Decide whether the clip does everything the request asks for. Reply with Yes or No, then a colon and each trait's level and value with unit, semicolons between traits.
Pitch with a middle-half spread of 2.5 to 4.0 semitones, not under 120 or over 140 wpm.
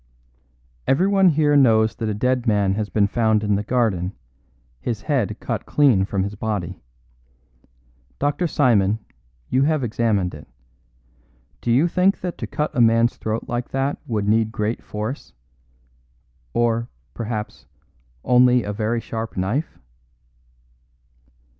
Yes: average, 3.7 semitones; slow, 135 wpm